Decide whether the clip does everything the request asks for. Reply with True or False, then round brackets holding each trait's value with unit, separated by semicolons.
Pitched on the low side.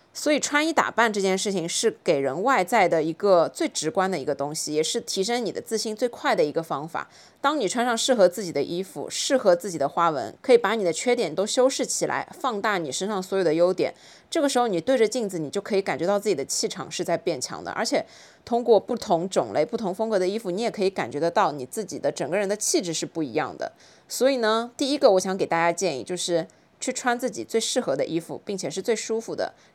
False (200 Hz)